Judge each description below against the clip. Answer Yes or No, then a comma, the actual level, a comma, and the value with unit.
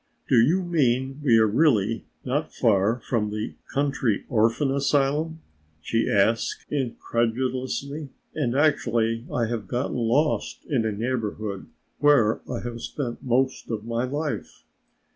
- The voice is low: Yes, low, 120 Hz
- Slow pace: Yes, slow, 130 wpm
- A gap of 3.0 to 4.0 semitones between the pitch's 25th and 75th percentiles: Yes, average, 3.7 semitones